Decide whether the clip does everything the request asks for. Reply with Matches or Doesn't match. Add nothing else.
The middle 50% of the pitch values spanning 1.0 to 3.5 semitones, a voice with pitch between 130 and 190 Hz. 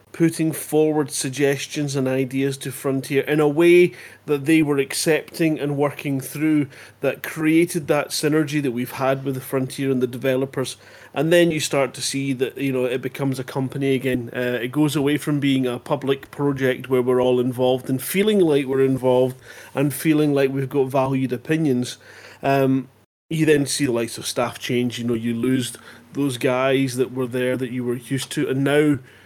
Matches